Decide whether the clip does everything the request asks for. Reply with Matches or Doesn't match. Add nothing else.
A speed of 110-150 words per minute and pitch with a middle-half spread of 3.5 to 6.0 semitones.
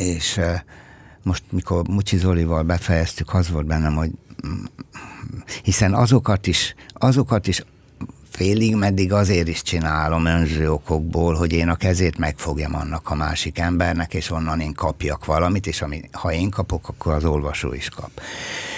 Doesn't match